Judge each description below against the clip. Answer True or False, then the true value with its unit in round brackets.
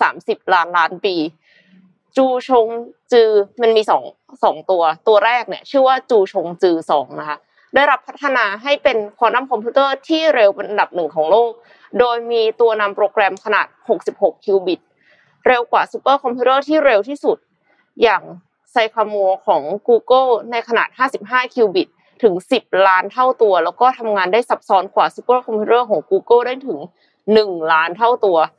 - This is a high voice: True (235 Hz)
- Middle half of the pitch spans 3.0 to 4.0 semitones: False (4.7 semitones)